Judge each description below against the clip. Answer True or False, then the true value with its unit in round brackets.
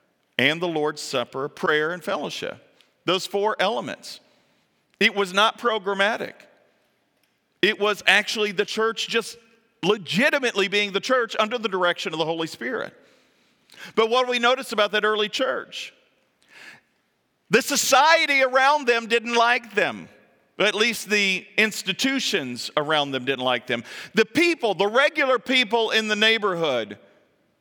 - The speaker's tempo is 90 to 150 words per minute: True (140 wpm)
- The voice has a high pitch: True (215 Hz)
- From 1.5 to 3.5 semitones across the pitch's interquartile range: False (4.2 semitones)